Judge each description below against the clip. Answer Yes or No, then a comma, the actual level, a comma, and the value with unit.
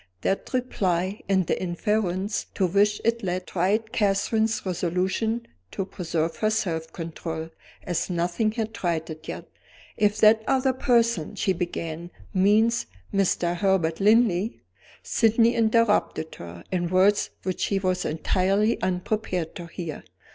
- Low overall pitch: No, high, 190 Hz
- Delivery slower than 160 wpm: Yes, slow, 135 wpm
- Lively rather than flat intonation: No, average, 4.0 semitones